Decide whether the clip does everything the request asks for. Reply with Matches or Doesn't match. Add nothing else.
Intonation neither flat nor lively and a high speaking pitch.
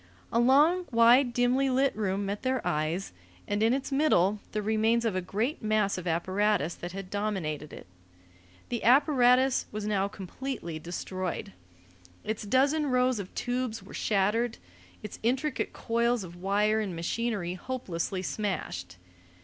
Matches